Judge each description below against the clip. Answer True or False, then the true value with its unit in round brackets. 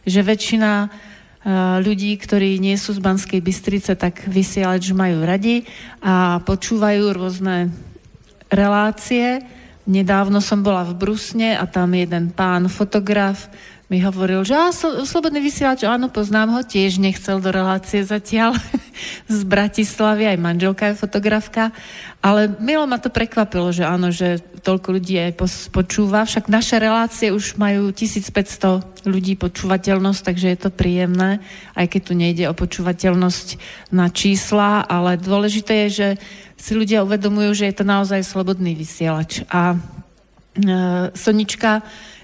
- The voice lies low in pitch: False (200 Hz)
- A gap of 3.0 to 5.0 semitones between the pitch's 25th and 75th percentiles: False (2.4 semitones)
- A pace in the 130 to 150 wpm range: True (140 wpm)